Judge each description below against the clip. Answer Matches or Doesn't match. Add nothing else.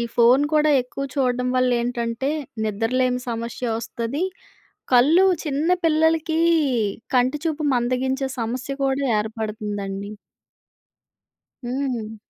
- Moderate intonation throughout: Matches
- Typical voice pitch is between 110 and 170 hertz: Doesn't match